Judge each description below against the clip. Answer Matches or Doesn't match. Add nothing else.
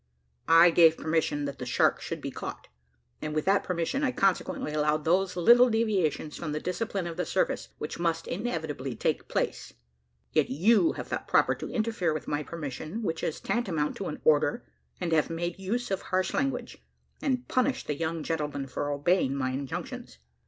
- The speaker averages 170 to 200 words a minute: Matches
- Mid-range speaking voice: Matches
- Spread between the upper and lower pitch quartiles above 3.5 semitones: Matches